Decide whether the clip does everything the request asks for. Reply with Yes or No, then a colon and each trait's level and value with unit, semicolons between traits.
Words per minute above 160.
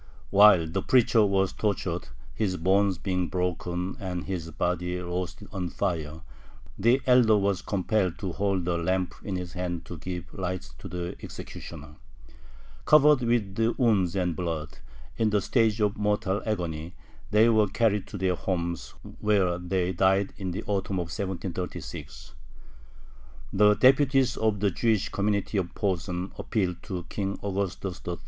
No: average, 150 wpm